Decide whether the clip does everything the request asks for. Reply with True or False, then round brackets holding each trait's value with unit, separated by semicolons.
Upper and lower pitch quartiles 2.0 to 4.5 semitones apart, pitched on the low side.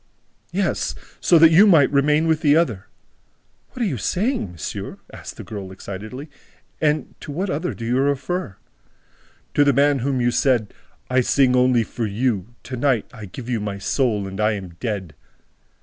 False (5.6 semitones; 125 Hz)